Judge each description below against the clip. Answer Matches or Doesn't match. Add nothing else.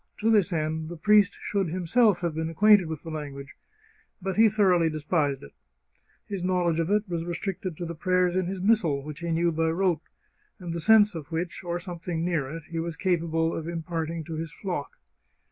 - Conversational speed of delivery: Doesn't match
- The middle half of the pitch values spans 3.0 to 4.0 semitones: Doesn't match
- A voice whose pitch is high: Doesn't match